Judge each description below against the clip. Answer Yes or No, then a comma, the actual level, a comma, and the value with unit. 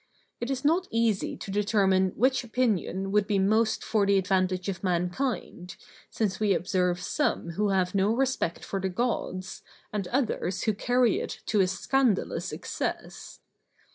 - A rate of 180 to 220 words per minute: No, average, 155 wpm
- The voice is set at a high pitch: Yes, high, 200 Hz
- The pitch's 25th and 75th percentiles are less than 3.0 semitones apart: No, average, 3.7 semitones